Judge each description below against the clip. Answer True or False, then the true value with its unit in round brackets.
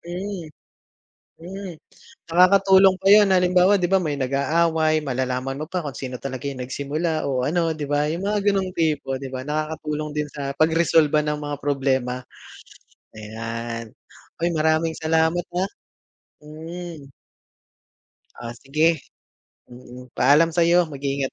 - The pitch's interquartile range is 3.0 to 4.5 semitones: True (4.0 semitones)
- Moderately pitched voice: True (155 Hz)